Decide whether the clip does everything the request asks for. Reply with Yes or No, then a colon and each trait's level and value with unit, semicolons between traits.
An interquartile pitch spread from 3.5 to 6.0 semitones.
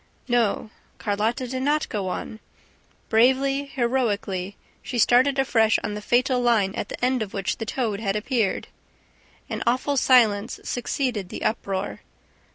Yes: average, 3.8 semitones